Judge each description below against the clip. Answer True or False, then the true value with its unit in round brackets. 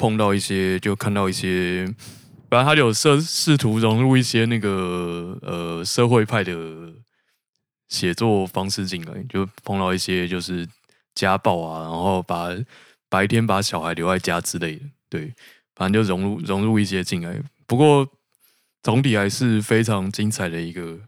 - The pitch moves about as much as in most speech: True (4.1 semitones)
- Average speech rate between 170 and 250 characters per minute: True (235 characters per minute)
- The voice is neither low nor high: False (100 Hz)